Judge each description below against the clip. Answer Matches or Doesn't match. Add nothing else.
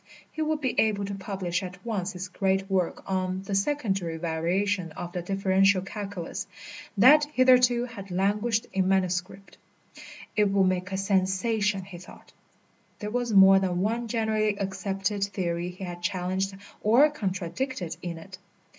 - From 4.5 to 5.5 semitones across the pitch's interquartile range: Doesn't match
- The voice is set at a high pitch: Matches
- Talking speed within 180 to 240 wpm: Doesn't match